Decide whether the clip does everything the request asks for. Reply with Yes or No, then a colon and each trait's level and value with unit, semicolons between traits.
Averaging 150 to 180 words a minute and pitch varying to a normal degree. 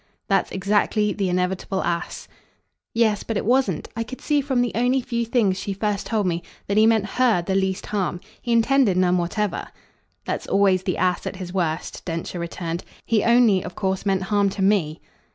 No: average, 190 wpm; average, 3.6 semitones